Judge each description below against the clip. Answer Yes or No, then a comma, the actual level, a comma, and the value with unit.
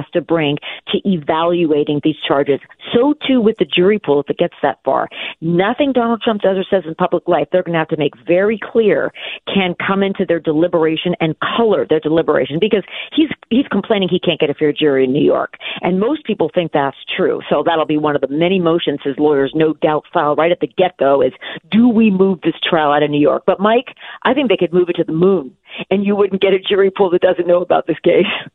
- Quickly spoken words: Yes, fast, 240 wpm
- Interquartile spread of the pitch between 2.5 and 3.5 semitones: No, average, 3.9 semitones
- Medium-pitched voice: Yes, medium, 175 Hz